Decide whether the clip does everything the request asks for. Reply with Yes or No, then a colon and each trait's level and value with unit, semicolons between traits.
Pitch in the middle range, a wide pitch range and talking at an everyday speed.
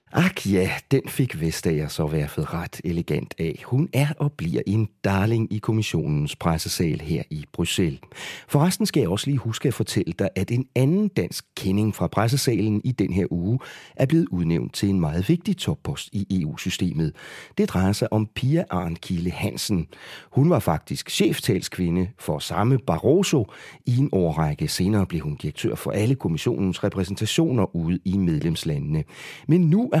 No: low, 105 Hz; wide, 7.6 semitones; average, 165 wpm